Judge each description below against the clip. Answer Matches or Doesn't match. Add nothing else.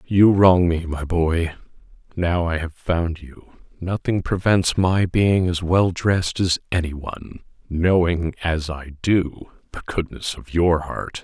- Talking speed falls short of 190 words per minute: Matches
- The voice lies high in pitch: Doesn't match